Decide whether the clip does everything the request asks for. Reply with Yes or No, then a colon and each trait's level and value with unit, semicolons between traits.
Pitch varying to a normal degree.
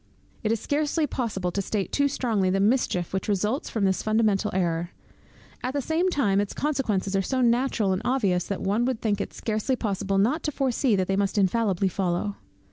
Yes: average, 4.8 semitones